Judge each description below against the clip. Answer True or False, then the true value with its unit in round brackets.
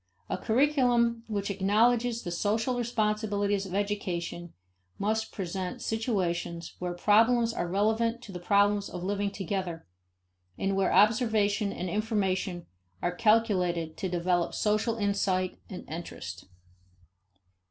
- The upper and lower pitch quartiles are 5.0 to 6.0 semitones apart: False (3.4 semitones)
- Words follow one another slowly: True (120 wpm)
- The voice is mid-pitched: False (205 Hz)